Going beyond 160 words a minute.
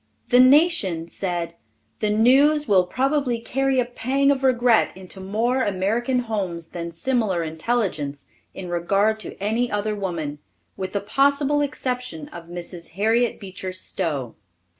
No: average, 140 wpm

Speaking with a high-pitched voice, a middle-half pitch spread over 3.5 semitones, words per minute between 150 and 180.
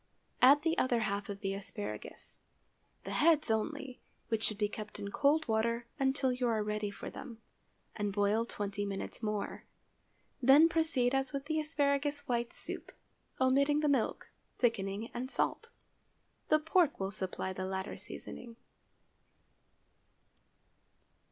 No: high, 240 Hz; average, 5.3 semitones; slow, 135 wpm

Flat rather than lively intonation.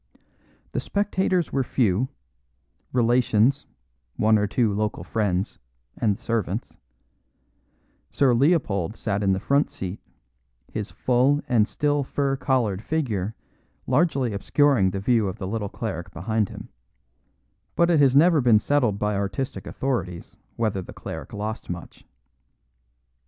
No: average, 5.3 semitones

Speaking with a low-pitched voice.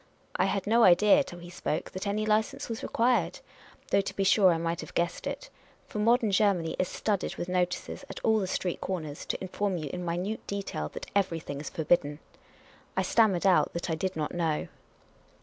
No: medium, 185 Hz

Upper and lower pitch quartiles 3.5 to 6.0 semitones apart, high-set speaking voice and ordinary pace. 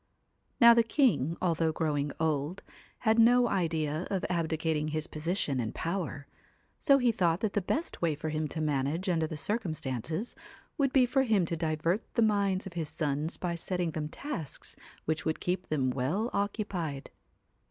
No: average, 4.8 semitones; medium, 165 Hz; average, 170 wpm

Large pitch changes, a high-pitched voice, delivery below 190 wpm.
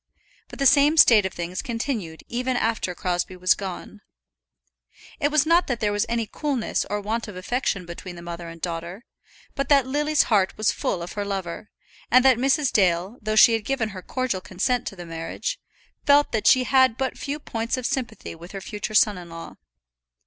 No: wide, 6.0 semitones; high, 215 Hz; average, 200 wpm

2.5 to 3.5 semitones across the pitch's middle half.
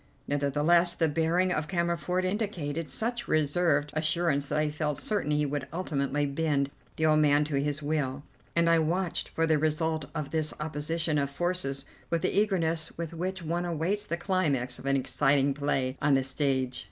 Yes: average, 2.9 semitones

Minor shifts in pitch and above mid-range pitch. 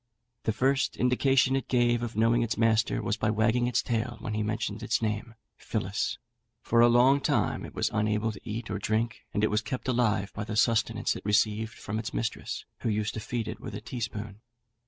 No: narrow, 2.0 semitones; low, 110 Hz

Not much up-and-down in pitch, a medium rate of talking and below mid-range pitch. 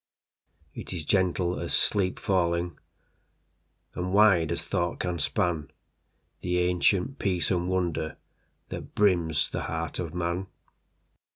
No: narrow, 1.5 semitones; slow, 105 wpm; very low, 90 Hz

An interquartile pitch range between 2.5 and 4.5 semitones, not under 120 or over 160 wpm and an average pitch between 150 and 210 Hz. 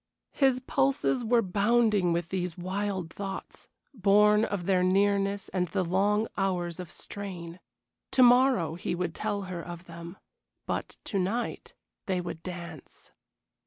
Yes: average, 3.0 semitones; average, 140 wpm; high, 190 Hz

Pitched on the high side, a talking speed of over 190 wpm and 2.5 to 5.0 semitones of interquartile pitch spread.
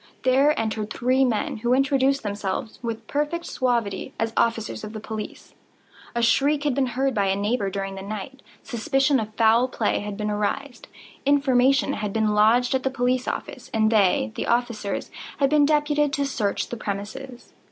No: high, 240 Hz; average, 175 wpm; average, 4.1 semitones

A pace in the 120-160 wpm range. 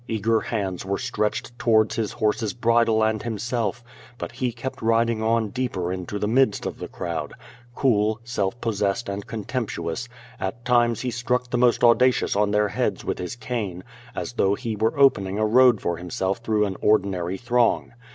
No: average, 175 wpm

